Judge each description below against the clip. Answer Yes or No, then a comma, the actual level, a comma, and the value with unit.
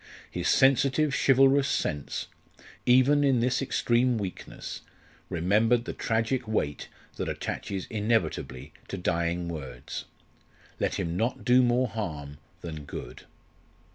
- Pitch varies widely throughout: Yes, wide, 7.2 semitones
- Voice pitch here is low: Yes, low, 110 Hz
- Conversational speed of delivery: No, slow, 115 wpm